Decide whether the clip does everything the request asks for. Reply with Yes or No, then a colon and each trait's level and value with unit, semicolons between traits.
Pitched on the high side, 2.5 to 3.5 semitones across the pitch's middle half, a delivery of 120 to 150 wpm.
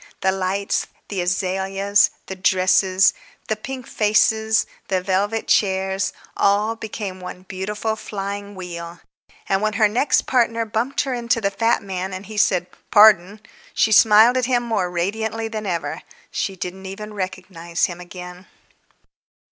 Yes: high, 200 Hz; average, 2.8 semitones; average, 145 wpm